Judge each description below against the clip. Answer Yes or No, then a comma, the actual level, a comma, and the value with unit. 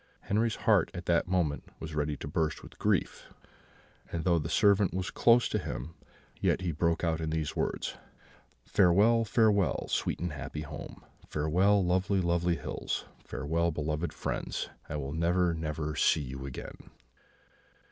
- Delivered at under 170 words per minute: Yes, average, 155 wpm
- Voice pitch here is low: Yes, very low, 85 Hz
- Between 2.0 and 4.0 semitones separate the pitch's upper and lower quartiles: Yes, average, 3.4 semitones